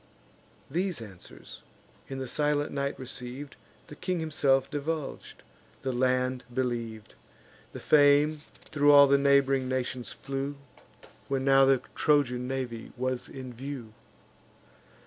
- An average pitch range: No, narrow, 2.1 semitones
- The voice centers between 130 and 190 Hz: Yes, low, 135 Hz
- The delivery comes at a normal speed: No, slow, 120 wpm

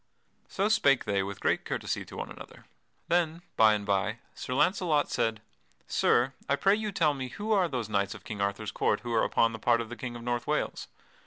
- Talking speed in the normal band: No, fast, 220 wpm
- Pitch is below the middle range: Yes, low, 120 Hz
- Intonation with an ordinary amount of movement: No, wide, 6.8 semitones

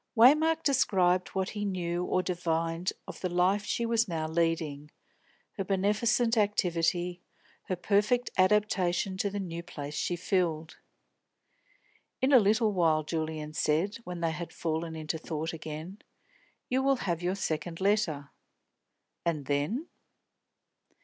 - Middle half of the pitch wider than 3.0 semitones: Yes, average, 4.0 semitones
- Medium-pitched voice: Yes, medium, 180 Hz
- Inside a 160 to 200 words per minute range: No, slow, 135 wpm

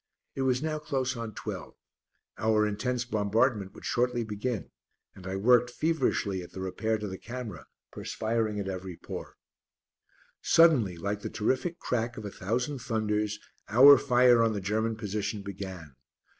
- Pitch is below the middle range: Yes, low, 110 Hz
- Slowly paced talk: No, average, 155 wpm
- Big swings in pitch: No, average, 3.5 semitones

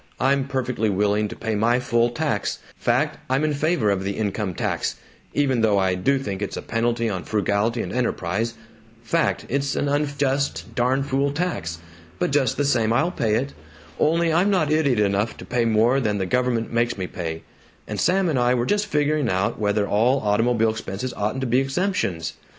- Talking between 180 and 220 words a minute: Yes, average, 190 wpm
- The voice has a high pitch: No, low, 120 Hz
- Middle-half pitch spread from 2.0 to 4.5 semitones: No, average, 4.9 semitones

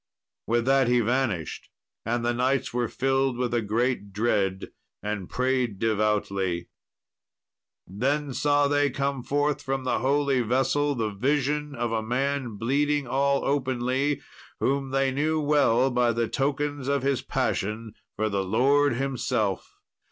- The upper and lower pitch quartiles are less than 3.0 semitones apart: No, average, 3.6 semitones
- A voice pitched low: Yes, low, 130 Hz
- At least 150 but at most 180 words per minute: No, average, 140 wpm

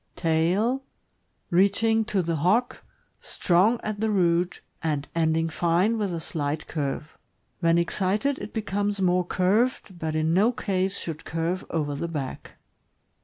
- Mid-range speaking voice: Yes, medium, 180 Hz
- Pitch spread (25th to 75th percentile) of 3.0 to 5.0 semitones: Yes, average, 4.0 semitones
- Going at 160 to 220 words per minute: No, average, 145 wpm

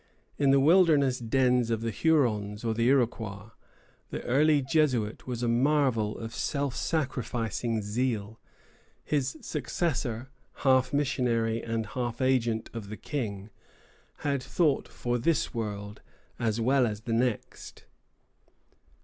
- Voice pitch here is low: Yes, low, 120 Hz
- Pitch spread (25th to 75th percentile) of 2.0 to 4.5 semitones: Yes, average, 3.4 semitones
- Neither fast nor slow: No, slow, 125 wpm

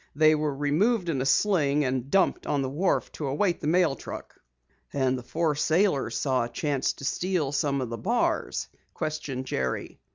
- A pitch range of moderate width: Yes, average, 4.1 semitones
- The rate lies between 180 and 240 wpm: Yes, average, 185 wpm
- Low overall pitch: No, medium, 145 Hz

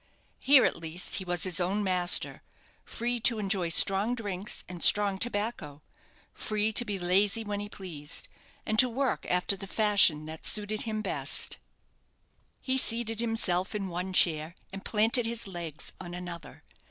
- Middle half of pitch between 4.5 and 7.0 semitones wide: No, average, 3.8 semitones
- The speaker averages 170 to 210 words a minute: No, average, 160 wpm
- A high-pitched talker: Yes, high, 200 Hz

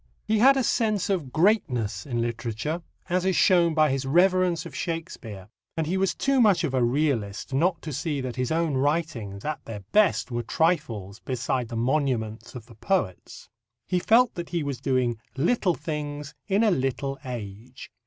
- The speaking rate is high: No, average, 180 wpm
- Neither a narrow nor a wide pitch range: No, wide, 6.6 semitones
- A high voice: No, medium, 145 Hz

